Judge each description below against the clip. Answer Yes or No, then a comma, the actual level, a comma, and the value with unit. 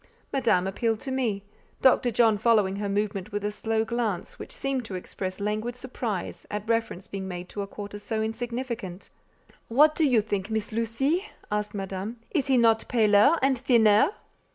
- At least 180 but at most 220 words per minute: No, average, 170 wpm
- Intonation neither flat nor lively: Yes, average, 3.0 semitones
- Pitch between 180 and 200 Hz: No, high, 220 Hz